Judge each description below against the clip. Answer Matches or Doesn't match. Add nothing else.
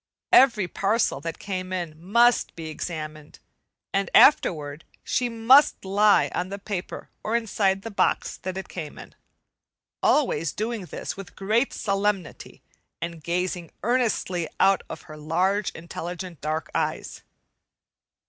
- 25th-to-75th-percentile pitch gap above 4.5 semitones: Doesn't match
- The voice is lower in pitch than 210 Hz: Matches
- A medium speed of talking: Doesn't match